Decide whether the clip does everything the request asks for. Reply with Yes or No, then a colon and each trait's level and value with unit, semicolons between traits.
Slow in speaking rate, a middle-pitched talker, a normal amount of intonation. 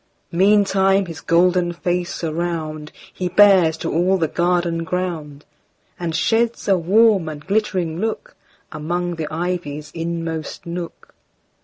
No: slow, 110 wpm; medium, 175 Hz; narrow, 2.3 semitones